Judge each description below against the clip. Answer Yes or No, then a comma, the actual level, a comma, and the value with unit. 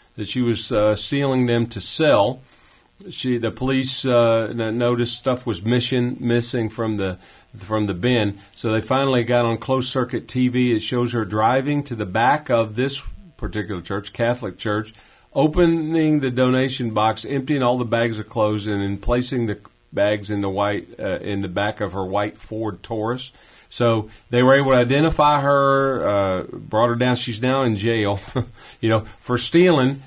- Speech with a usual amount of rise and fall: Yes, average, 3.2 semitones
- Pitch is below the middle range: Yes, low, 120 Hz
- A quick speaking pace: No, average, 180 wpm